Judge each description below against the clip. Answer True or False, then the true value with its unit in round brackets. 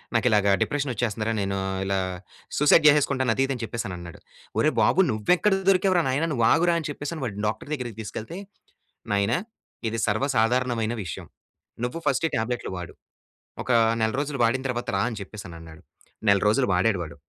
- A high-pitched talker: False (115 Hz)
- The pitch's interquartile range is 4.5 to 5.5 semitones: True (5.1 semitones)